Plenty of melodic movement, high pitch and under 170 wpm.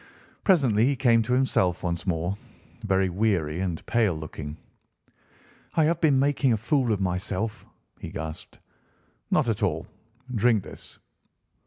No: wide, 6.0 semitones; low, 105 Hz; average, 140 wpm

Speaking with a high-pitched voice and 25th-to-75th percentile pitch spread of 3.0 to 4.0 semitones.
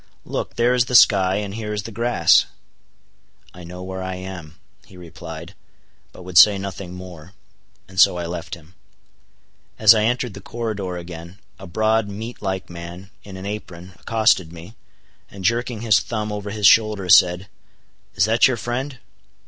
No: very low, 95 Hz; average, 3.5 semitones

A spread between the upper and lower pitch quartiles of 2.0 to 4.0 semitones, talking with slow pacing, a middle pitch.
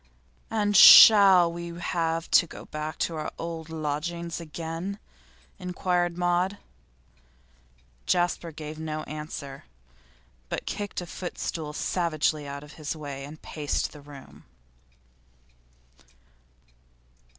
Yes: narrow, 2.5 semitones; slow, 105 wpm; medium, 165 Hz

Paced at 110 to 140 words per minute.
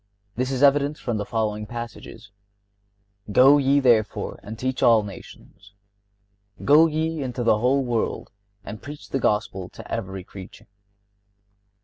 Yes: slow, 135 wpm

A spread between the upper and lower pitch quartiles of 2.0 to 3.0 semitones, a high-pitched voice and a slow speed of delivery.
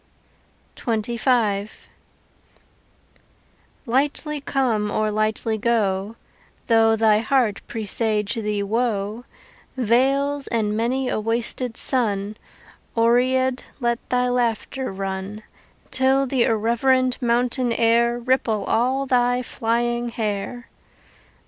Yes: average, 2.7 semitones; high, 235 Hz; slow, 90 wpm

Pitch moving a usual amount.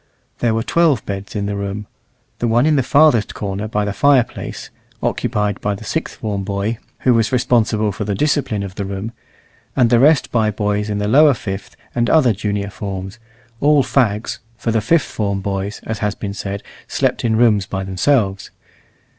Yes: average, 3.2 semitones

